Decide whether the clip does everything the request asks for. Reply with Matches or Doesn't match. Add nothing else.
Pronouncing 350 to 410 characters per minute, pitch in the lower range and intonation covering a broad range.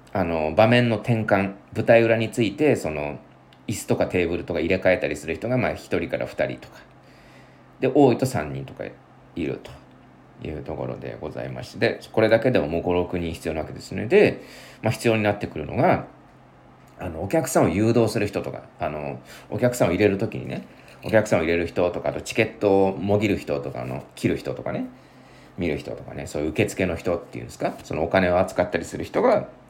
Matches